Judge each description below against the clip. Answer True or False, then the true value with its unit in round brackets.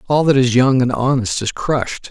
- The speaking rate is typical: False (230 wpm)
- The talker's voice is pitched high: False (125 Hz)